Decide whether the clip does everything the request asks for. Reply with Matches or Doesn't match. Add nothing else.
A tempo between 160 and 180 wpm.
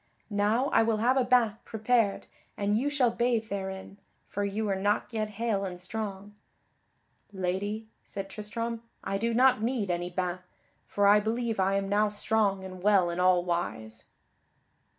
Matches